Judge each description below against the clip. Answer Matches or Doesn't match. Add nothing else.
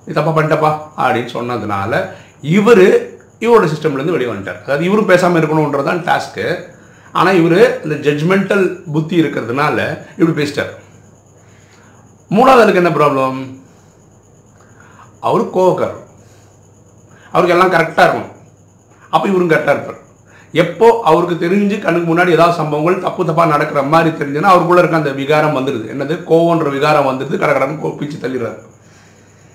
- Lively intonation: Matches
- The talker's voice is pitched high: Doesn't match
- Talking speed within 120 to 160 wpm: Matches